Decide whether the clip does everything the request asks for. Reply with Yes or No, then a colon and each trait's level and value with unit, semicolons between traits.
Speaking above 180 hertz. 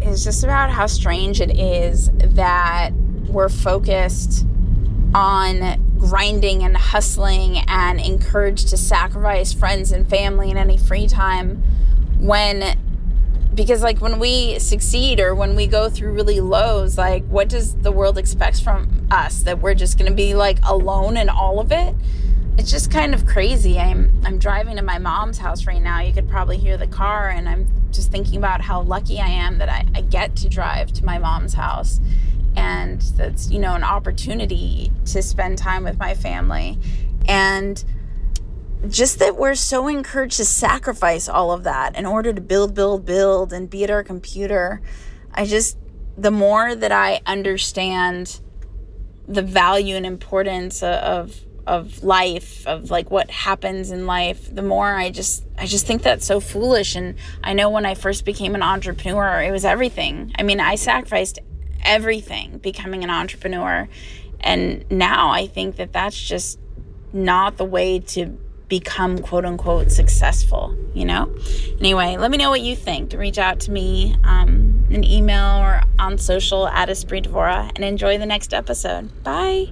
Yes: high, 190 Hz